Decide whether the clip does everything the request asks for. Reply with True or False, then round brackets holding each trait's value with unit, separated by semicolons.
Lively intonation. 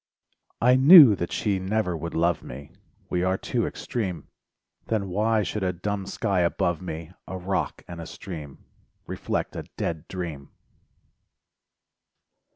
False (3.4 semitones)